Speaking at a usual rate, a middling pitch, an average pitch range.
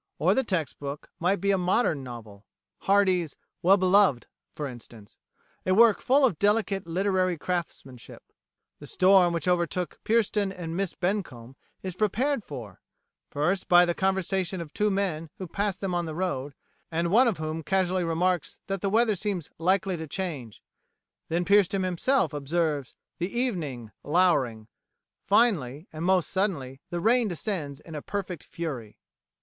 Yes: average, 155 wpm; medium, 180 Hz; average, 4.2 semitones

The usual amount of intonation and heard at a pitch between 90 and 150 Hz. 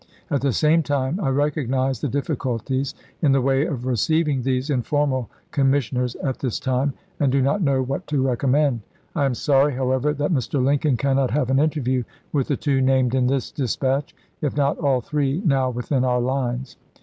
No: narrow, 2.0 semitones; low, 135 Hz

